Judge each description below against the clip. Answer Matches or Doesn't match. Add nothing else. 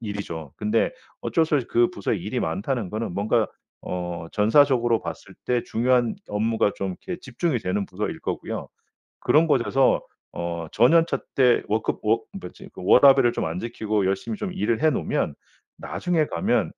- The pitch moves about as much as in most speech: Matches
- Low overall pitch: Matches